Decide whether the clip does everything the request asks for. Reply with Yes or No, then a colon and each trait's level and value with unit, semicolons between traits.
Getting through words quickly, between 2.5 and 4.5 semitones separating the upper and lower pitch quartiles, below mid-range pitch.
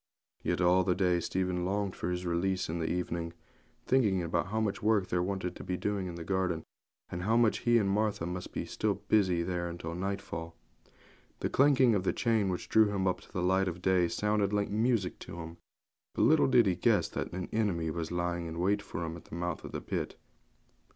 Yes: fast, 210 wpm; average, 2.9 semitones; very low, 95 Hz